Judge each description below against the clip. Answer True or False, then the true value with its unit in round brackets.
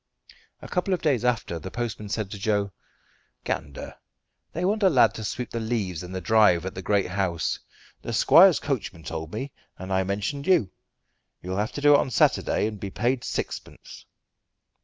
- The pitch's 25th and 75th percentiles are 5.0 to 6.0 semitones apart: True (5.4 semitones)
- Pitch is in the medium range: False (105 Hz)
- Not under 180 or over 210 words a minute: True (185 wpm)